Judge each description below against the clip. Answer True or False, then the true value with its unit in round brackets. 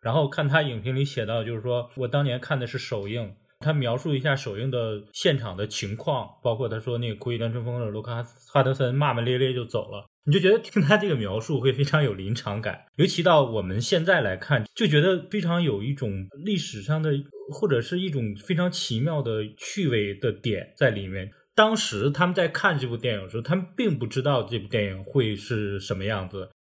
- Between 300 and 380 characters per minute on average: True (320 characters per minute)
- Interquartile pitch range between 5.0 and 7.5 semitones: True (5.6 semitones)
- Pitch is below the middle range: True (125 Hz)